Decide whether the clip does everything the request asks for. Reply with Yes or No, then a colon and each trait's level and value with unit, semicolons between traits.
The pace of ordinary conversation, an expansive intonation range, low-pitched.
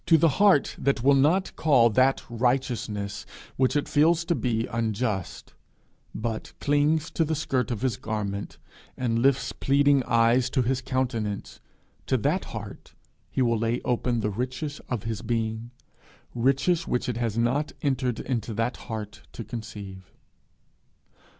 No: average, 145 wpm; average, 3.5 semitones; low, 125 Hz